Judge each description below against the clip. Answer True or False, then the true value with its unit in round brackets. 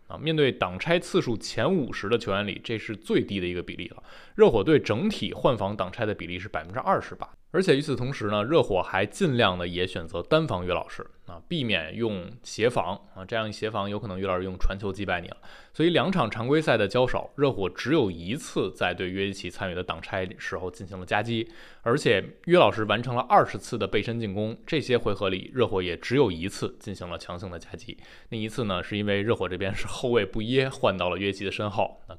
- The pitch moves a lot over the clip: False (3.9 semitones)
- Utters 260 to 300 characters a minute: False (340 characters per minute)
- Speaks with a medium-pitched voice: False (105 Hz)